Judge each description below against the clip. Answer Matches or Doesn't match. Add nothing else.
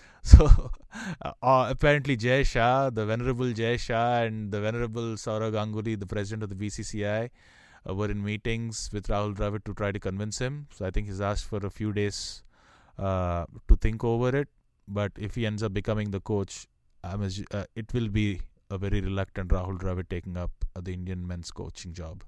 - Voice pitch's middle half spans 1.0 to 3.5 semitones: Matches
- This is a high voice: Doesn't match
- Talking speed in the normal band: Matches